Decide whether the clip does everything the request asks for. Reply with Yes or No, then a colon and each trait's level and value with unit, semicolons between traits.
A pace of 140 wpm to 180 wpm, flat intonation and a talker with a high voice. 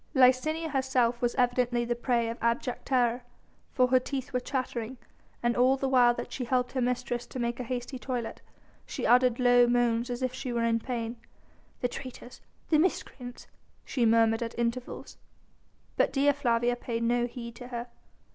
Yes: average, 175 wpm; narrow, 1.3 semitones; high, 245 Hz